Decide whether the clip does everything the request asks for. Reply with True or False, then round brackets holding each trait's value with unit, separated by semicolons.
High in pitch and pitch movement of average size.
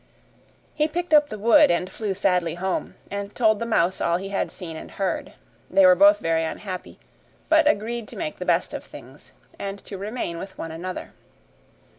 True (200 Hz; 5.0 semitones)